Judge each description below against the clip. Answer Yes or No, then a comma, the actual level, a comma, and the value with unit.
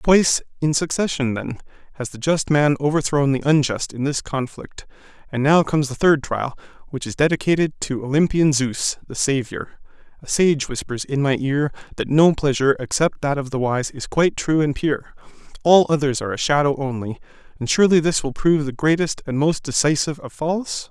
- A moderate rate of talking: Yes, average, 185 wpm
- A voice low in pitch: No, medium, 145 Hz